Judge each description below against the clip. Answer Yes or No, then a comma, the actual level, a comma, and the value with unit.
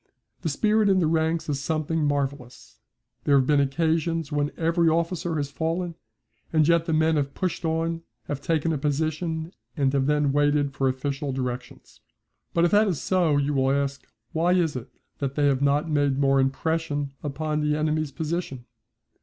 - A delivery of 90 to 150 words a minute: No, average, 175 wpm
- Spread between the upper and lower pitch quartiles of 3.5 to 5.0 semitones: No, average, 2.7 semitones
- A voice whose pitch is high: No, medium, 150 Hz